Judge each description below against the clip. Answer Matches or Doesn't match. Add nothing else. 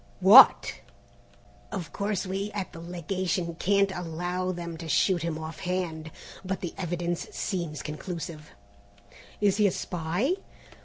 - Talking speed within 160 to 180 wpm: Doesn't match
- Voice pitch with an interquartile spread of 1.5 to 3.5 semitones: Matches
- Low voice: Doesn't match